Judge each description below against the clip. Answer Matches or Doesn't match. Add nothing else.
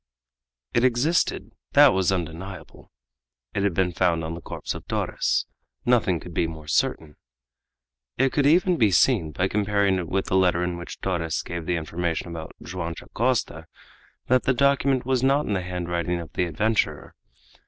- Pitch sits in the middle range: Doesn't match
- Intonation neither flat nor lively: Doesn't match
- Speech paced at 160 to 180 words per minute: Matches